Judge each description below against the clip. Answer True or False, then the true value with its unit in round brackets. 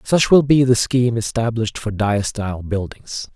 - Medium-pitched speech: False (115 Hz)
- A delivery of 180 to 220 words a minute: False (160 wpm)